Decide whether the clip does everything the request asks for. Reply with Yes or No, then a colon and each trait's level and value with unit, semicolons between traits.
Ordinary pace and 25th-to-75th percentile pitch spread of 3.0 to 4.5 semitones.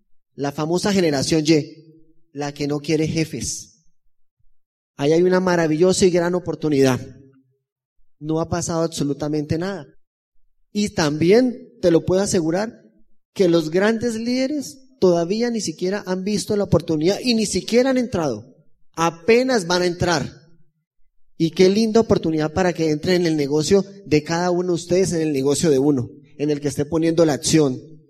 Yes: average, 160 wpm; average, 3.9 semitones